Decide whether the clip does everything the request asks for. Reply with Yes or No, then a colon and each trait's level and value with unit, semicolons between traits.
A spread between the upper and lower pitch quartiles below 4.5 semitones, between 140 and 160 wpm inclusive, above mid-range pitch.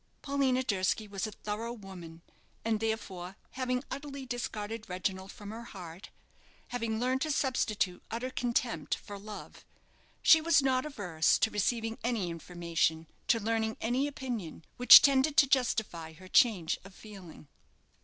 No: average, 5.1 semitones; average, 145 wpm; high, 220 Hz